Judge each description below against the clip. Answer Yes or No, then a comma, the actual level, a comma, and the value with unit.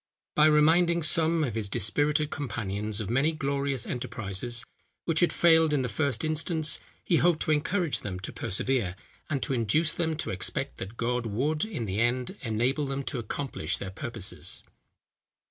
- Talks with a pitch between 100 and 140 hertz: Yes, low, 135 Hz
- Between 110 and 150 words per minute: No, average, 165 wpm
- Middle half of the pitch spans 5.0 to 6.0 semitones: Yes, wide, 5.5 semitones